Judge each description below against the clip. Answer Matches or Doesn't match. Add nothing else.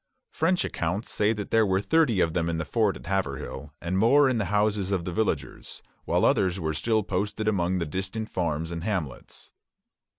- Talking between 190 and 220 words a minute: Matches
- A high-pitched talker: Doesn't match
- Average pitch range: Matches